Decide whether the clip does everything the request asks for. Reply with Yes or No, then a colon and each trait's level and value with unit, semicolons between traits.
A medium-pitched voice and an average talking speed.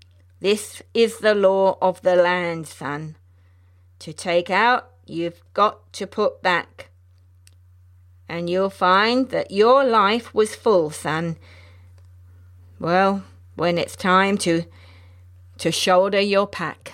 No: medium, 165 Hz; slow, 120 wpm